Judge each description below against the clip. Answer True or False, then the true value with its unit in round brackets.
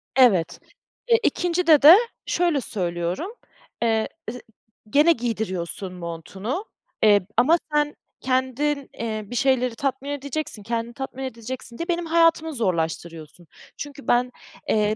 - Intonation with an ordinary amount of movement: False (5.9 semitones)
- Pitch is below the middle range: False (250 Hz)